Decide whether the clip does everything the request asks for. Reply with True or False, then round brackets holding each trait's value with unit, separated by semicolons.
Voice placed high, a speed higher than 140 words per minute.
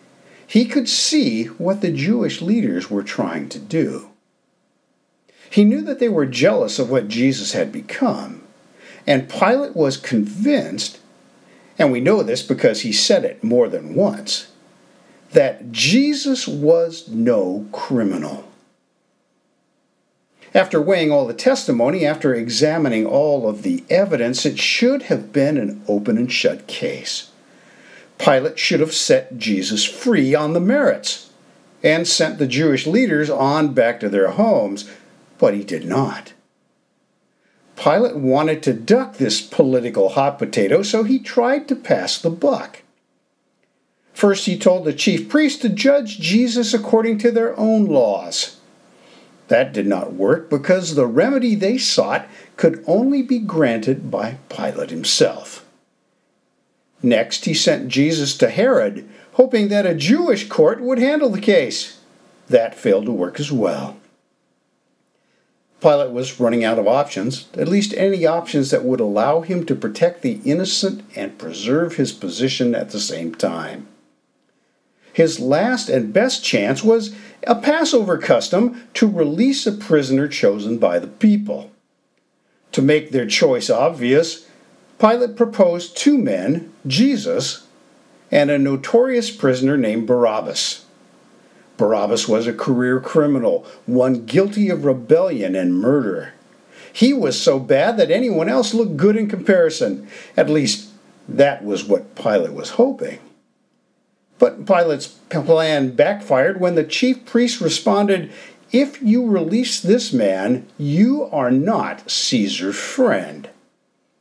False (200 Hz; 135 wpm)